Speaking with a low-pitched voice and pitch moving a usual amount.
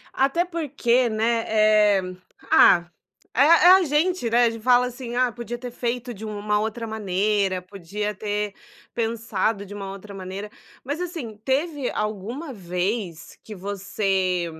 No: high, 220 Hz; average, 3.6 semitones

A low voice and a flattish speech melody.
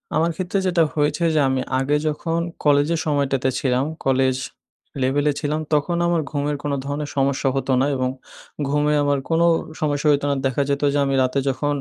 No: medium, 145 Hz; narrow, 1.9 semitones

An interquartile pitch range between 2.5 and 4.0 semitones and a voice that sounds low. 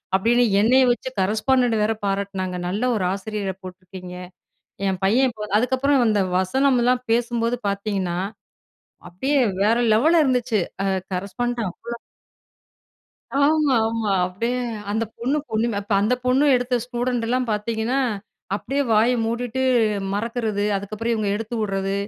No: average, 3.7 semitones; high, 230 Hz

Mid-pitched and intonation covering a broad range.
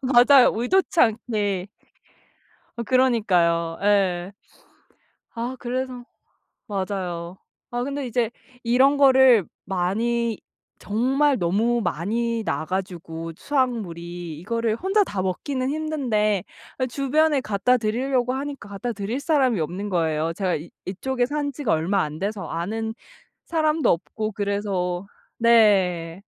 No: high, 220 Hz; wide, 5.7 semitones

